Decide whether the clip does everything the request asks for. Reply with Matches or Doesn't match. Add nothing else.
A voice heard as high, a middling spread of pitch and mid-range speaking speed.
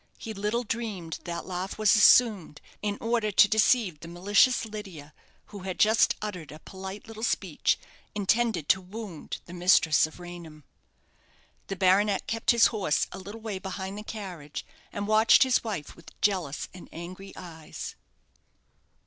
Matches